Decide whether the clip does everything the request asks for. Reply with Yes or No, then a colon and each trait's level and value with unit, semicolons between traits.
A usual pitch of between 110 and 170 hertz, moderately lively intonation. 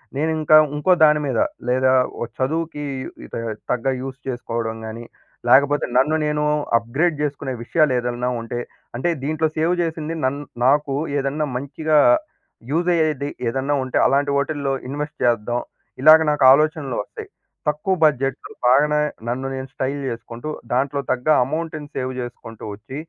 Yes: medium, 140 Hz; average, 3.0 semitones